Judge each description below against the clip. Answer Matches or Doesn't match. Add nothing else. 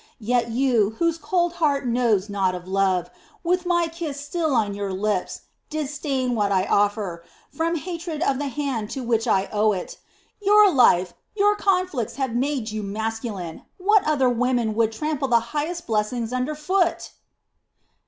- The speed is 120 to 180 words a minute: Matches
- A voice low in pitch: Doesn't match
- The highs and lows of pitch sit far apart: Matches